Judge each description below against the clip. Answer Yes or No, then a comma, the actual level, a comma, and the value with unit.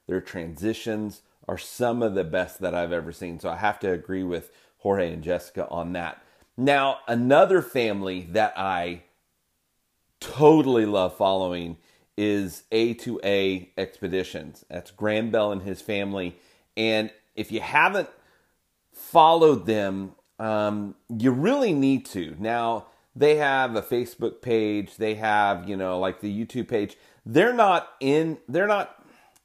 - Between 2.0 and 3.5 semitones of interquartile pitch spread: No, average, 4.2 semitones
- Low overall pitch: Yes, low, 105 Hz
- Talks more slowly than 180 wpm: Yes, average, 140 wpm